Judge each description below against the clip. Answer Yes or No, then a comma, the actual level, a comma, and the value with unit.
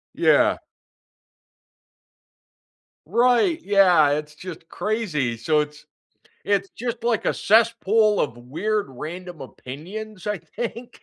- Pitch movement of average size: No, wide, 6.4 semitones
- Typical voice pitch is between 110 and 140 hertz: No, high, 190 Hz